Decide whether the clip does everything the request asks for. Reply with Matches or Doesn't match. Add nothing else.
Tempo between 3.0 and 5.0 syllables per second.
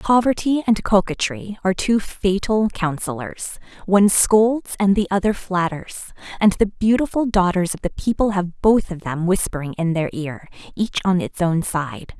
Matches